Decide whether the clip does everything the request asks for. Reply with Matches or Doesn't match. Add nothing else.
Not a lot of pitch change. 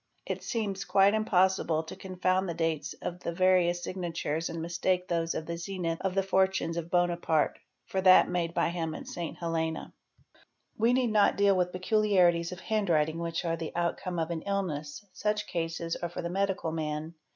Matches